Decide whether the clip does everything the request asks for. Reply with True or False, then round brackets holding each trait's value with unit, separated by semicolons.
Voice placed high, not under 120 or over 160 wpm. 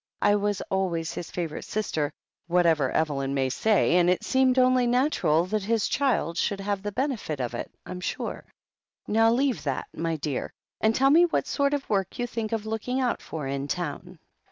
False (200 Hz; 190 wpm)